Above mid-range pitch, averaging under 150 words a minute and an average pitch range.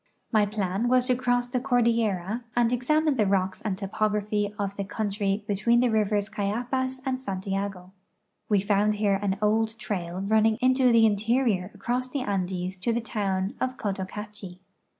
No: high, 210 Hz; average, 160 wpm; average, 3.5 semitones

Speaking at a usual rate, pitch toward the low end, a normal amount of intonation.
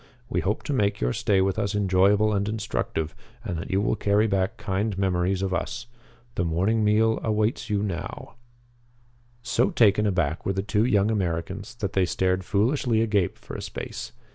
No: average, 180 wpm; low, 100 Hz; narrow, 2.3 semitones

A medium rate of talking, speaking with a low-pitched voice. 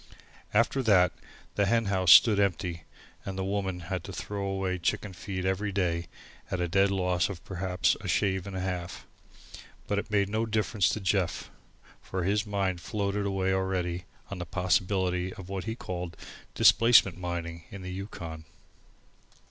Yes: average, 170 wpm; very low, 95 Hz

